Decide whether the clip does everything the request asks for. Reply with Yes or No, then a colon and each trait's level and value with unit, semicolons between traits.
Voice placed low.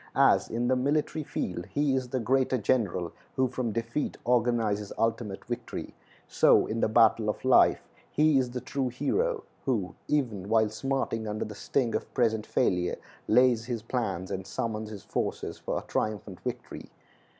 Yes: low, 115 Hz